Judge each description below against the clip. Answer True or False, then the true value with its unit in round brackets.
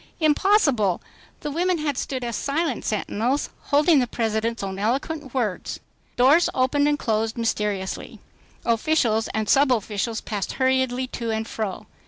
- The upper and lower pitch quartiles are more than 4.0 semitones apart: True (4.8 semitones)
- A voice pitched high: True (245 Hz)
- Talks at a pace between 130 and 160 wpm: True (135 wpm)